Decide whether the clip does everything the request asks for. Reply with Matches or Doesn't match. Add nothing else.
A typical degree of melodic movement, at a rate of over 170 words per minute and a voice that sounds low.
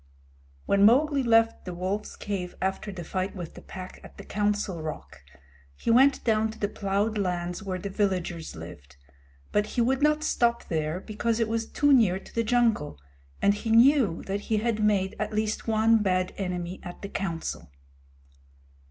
Doesn't match